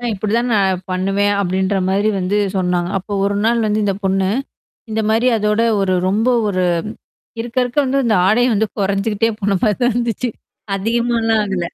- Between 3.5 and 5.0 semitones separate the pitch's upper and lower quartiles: No, average, 2.9 semitones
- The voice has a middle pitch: No, high, 205 Hz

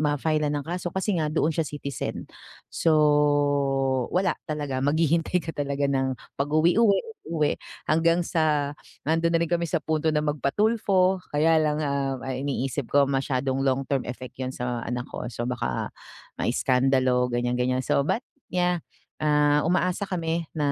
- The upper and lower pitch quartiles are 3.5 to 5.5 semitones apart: Yes, average, 3.8 semitones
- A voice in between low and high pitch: Yes, medium, 150 Hz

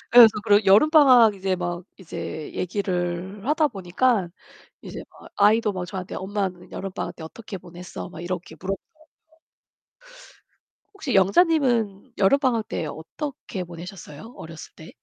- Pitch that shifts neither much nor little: Yes, average, 4.5 semitones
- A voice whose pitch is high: Yes, high, 195 Hz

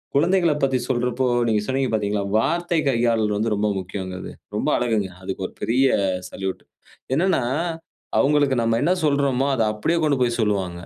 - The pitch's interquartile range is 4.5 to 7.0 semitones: Yes, average, 5.0 semitones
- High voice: No, low, 120 Hz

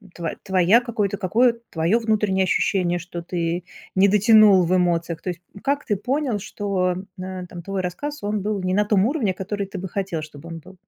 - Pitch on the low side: No, high, 190 Hz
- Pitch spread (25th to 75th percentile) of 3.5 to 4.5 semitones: No, average, 2.9 semitones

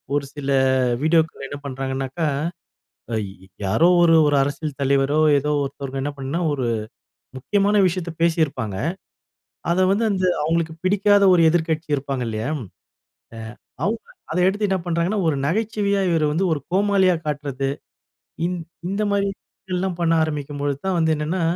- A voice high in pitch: No, medium, 160 Hz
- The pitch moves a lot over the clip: No, average, 5.0 semitones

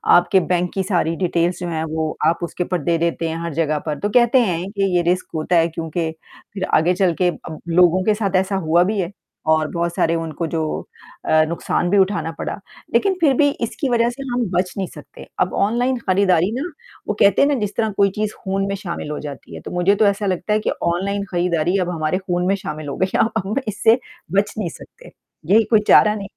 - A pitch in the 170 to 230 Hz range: Yes, medium, 185 Hz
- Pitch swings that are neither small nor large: Yes, average, 3.4 semitones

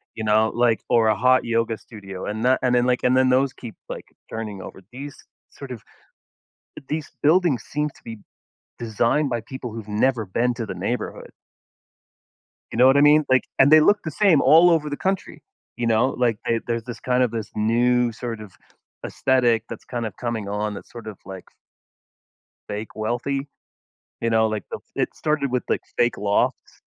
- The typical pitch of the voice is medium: No, low, 120 Hz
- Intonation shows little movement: No, average, 3.1 semitones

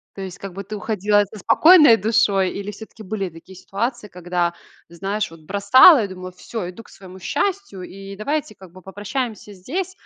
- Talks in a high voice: Yes, high, 200 Hz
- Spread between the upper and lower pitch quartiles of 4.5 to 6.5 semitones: No, average, 3.2 semitones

